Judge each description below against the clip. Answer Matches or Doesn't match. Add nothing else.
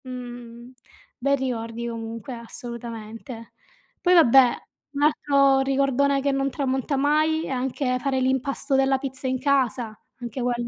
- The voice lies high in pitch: Matches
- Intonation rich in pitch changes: Doesn't match